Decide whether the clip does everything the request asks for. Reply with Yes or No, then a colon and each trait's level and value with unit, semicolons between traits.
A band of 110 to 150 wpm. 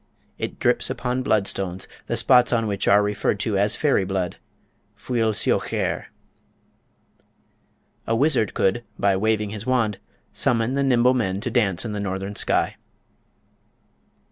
Yes: average, 140 wpm